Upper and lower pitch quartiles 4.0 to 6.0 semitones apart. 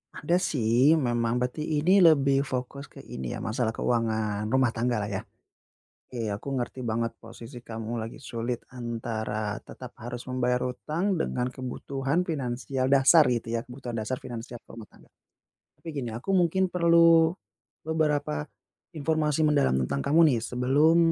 Yes: average, 4.5 semitones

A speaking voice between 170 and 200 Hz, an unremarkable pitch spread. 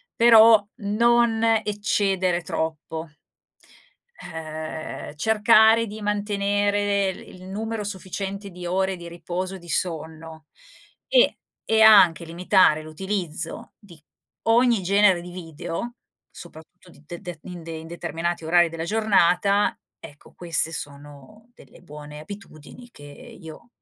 Yes: medium, 185 Hz; average, 4.2 semitones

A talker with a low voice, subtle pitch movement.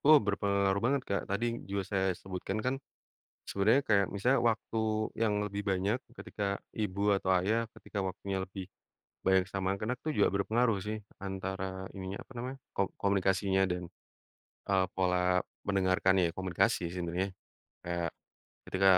Yes: low, 100 Hz; narrow, 1.7 semitones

